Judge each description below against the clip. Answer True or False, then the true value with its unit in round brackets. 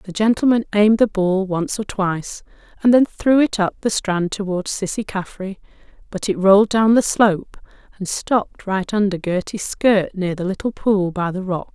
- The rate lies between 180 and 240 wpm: True (190 wpm)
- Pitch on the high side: True (200 Hz)